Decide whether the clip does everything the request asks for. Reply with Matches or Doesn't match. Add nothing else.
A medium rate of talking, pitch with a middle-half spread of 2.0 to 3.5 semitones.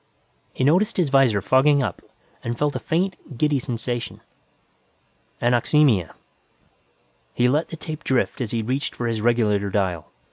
Doesn't match